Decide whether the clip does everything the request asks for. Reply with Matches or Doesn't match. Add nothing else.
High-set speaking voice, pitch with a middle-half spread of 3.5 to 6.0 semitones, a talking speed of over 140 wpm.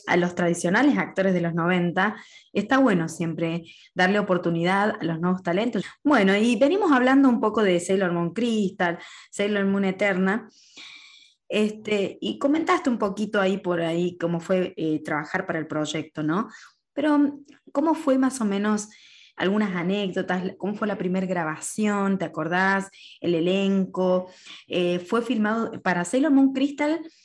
Matches